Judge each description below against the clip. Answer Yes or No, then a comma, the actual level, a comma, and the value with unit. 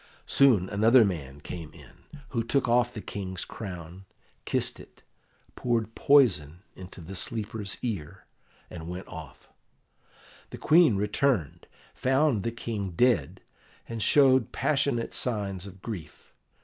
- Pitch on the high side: No, low, 105 Hz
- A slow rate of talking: Yes, slow, 125 wpm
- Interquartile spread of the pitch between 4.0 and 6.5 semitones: Yes, average, 5.2 semitones